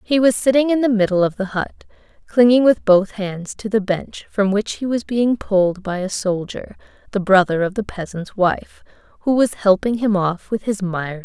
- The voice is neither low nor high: No, high, 205 Hz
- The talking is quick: Yes, fast, 215 wpm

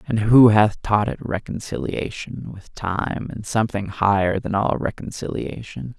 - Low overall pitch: Yes, low, 105 Hz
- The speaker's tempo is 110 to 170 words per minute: Yes, average, 140 wpm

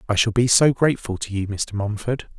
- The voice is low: Yes, low, 110 Hz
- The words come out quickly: Yes, fast, 225 wpm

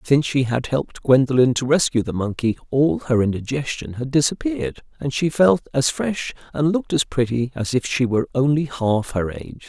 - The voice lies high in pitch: No, low, 125 Hz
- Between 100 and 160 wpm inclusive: No, average, 190 wpm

